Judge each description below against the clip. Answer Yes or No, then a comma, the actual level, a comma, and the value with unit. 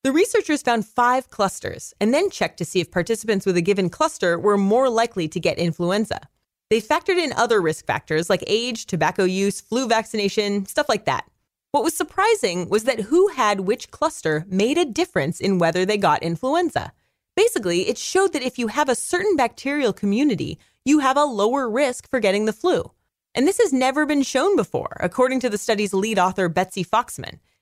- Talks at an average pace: Yes, average, 195 wpm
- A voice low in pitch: No, high, 225 Hz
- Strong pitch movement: Yes, wide, 7.4 semitones